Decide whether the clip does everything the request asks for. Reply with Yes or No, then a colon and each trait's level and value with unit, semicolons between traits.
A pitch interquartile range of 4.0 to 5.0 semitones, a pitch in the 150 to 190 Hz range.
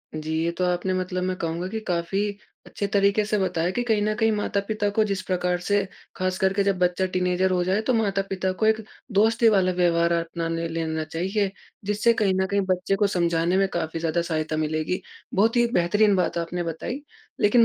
No: average, 3.2 semitones; medium, 185 Hz